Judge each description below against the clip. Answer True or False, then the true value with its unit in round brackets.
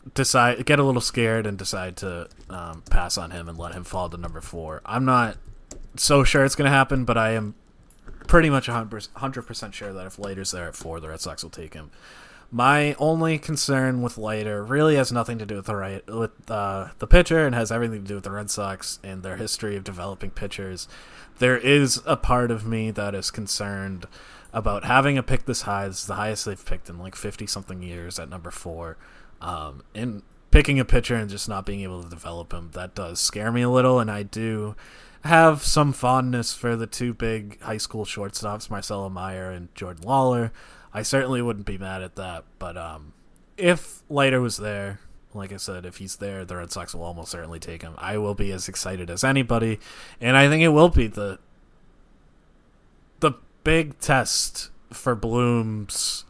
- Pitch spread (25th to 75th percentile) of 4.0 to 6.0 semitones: True (4.6 semitones)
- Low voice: True (105 Hz)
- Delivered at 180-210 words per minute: True (205 wpm)